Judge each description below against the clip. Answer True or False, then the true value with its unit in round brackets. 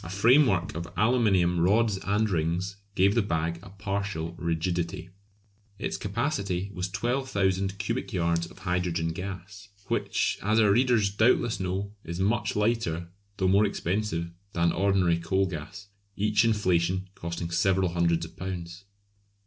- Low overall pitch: True (95 Hz)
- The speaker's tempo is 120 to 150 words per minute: True (140 wpm)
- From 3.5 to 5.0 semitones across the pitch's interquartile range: False (3.0 semitones)